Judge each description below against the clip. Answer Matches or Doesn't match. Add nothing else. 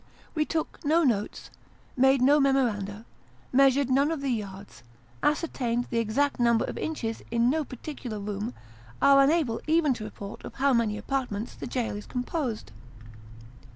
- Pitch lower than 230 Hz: Doesn't match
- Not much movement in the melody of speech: Doesn't match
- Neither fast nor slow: Matches